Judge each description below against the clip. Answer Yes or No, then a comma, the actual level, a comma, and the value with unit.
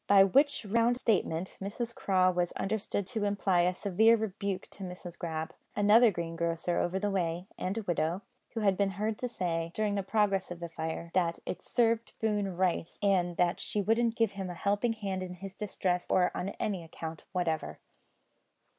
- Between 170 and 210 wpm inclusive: Yes, average, 180 wpm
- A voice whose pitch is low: No, high, 190 Hz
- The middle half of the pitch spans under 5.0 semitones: Yes, average, 3.1 semitones